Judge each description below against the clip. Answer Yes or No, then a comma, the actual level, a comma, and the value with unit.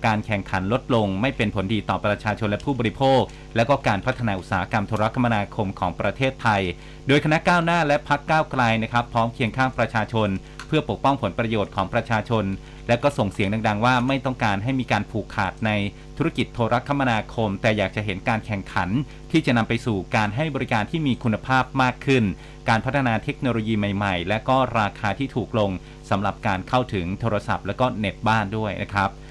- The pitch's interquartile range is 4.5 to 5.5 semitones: No, average, 4.1 semitones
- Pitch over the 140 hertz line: No, low, 115 Hz